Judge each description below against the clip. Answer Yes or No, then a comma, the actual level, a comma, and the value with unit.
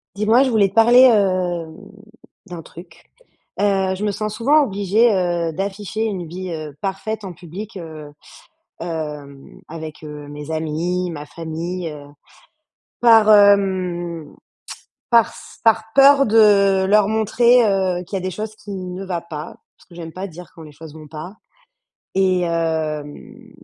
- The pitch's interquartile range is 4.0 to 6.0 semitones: Yes, average, 4.3 semitones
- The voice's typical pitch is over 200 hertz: No, medium, 185 Hz